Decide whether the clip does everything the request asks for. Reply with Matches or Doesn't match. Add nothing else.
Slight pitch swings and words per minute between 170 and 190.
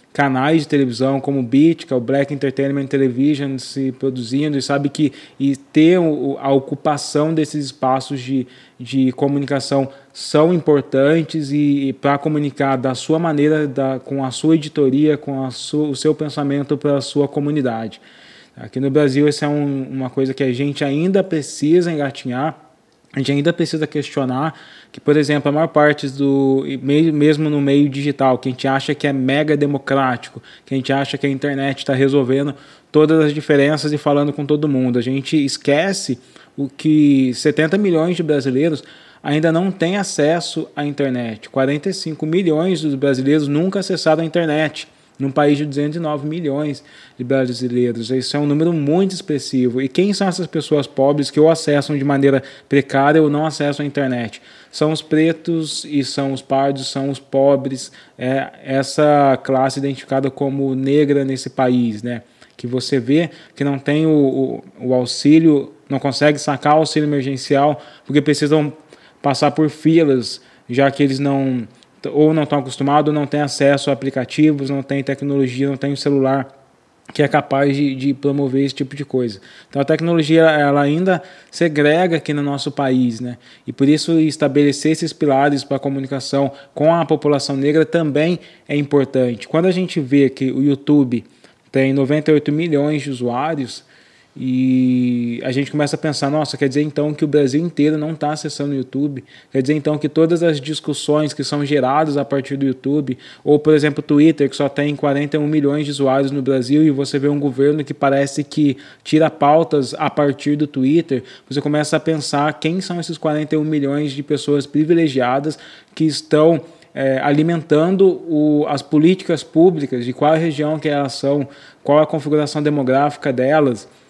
Matches